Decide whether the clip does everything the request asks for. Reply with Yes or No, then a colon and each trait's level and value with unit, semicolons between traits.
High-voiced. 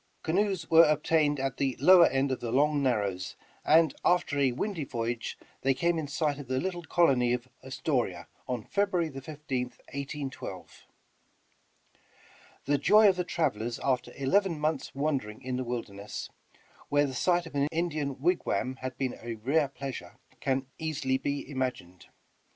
No: medium, 140 Hz